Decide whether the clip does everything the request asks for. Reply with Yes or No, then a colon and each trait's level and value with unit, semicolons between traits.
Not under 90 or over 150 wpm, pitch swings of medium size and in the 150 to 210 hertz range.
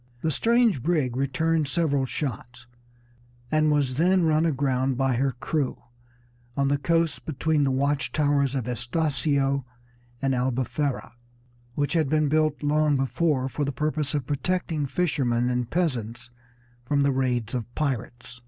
No: average, 145 wpm; average, 3.1 semitones; medium, 140 Hz